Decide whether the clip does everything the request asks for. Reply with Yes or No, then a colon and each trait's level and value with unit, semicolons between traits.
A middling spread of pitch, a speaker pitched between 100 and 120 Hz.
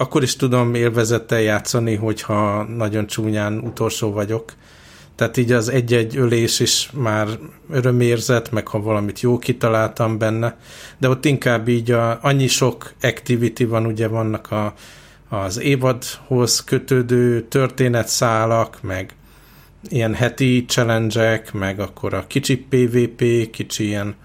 No: narrow, 2.2 semitones; low, 115 Hz